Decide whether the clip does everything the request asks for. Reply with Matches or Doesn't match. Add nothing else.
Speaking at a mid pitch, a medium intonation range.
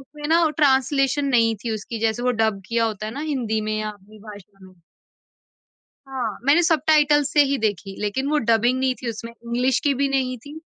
Doesn't match